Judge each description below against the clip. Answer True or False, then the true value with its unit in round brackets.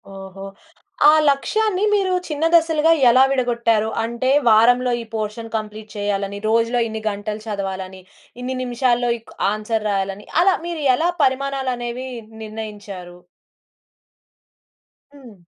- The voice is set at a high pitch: True (230 Hz)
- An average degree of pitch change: True (4.0 semitones)